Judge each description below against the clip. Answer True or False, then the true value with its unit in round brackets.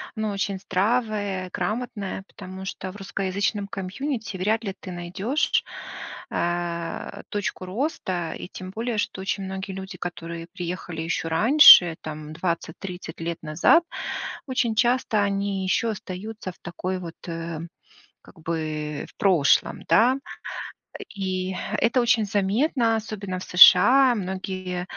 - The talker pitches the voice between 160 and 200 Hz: True (190 Hz)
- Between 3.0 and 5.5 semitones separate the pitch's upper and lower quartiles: True (3.4 semitones)